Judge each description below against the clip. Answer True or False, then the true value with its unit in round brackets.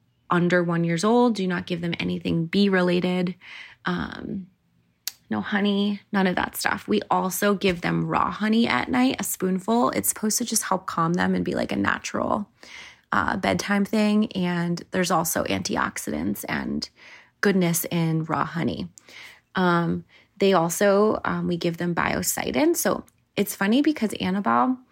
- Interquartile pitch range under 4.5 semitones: True (3.5 semitones)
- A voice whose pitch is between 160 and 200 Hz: True (185 Hz)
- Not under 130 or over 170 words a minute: True (155 wpm)